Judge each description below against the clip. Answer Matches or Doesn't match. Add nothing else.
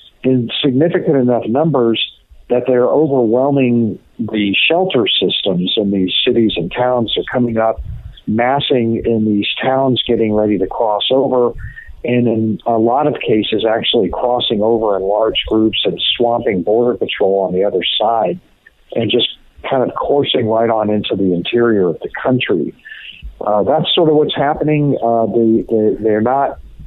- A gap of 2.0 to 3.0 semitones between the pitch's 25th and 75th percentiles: Matches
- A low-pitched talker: Matches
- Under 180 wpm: Matches